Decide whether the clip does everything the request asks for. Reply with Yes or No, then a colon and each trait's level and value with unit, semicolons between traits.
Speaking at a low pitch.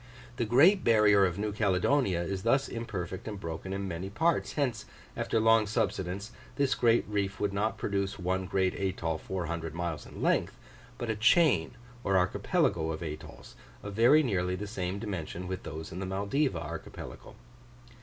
Yes: low, 100 Hz